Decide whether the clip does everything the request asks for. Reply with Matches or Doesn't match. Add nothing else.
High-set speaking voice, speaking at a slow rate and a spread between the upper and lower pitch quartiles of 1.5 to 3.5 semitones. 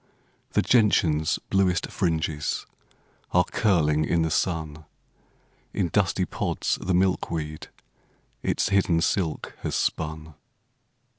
Doesn't match